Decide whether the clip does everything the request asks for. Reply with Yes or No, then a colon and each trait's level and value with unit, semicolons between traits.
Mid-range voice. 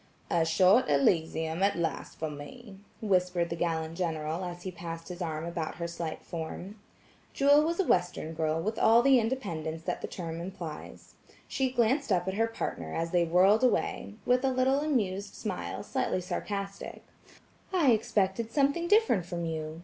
Yes: medium, 180 Hz